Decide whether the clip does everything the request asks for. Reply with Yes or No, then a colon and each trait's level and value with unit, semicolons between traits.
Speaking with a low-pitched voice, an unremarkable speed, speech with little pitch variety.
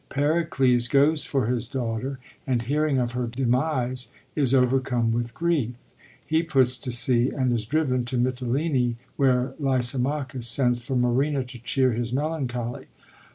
Yes: low, 130 Hz; average, 145 wpm; narrow, 2.2 semitones